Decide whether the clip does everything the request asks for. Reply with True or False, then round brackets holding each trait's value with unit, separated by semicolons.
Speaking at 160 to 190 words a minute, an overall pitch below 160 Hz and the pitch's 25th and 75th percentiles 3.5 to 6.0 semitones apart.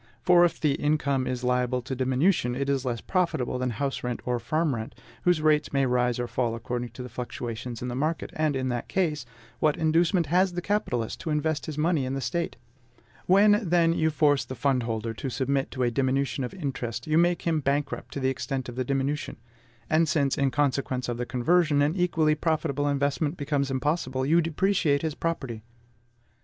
False (200 wpm; 140 Hz; 3.9 semitones)